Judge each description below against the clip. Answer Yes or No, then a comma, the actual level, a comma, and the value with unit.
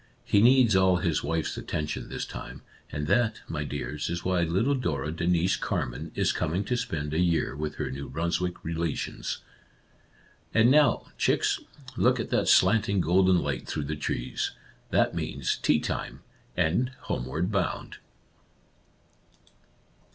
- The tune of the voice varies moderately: Yes, average, 4.8 semitones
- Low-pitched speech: Yes, very low, 85 Hz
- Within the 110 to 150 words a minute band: Yes, average, 145 wpm